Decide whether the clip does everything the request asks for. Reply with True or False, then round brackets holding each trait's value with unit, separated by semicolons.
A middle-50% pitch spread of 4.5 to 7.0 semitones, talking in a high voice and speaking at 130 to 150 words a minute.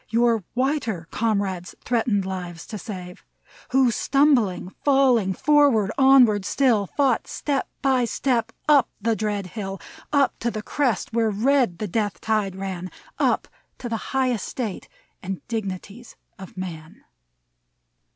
True (4.9 semitones; 220 Hz; 140 wpm)